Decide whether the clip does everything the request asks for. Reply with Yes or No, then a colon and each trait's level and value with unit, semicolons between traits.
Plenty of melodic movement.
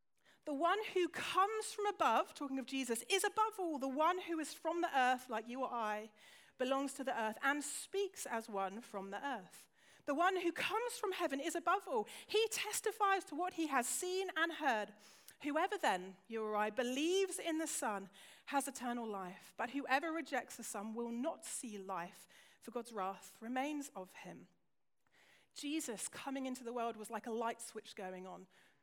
Yes: wide, 7.3 semitones